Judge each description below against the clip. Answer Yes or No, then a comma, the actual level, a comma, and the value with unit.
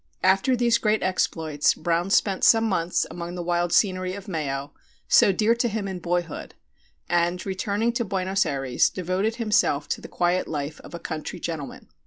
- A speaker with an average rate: Yes, average, 175 wpm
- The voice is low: No, medium, 185 Hz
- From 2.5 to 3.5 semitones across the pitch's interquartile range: Yes, average, 3.2 semitones